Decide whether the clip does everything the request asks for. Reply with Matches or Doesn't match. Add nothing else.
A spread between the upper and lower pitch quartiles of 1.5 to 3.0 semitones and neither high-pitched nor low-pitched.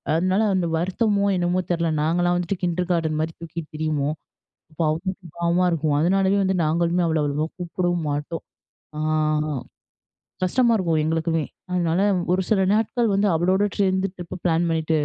Matches